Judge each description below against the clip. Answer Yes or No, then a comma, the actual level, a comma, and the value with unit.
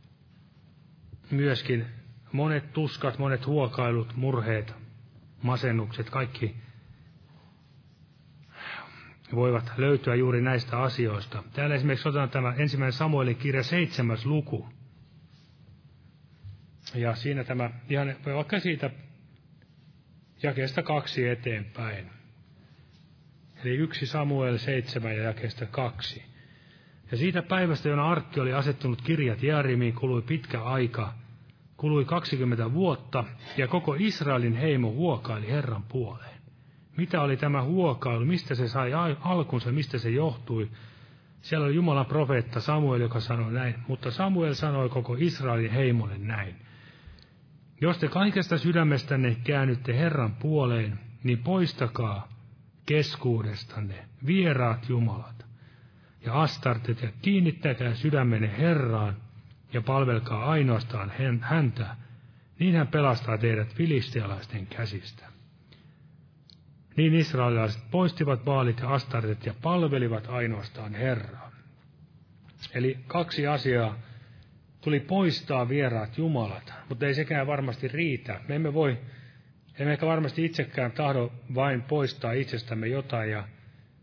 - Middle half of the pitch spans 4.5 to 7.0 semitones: No, average, 3.9 semitones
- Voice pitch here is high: No, low, 130 Hz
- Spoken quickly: No, average, 105 wpm